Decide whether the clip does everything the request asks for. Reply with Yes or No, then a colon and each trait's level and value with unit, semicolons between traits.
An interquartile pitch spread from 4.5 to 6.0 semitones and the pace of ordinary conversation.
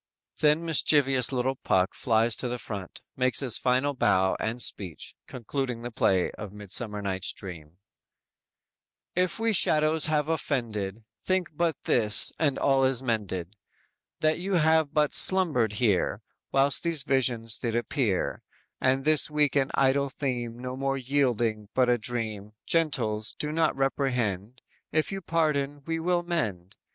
Yes: wide, 5.4 semitones; average, 150 wpm